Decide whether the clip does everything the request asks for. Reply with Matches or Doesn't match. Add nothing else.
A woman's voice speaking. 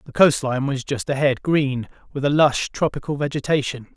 Doesn't match